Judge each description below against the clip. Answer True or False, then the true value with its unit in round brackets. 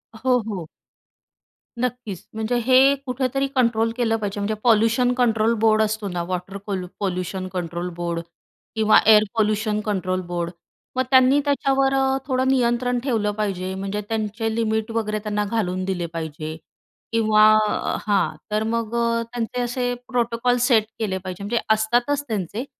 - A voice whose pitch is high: True (220 Hz)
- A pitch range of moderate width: True (3.6 semitones)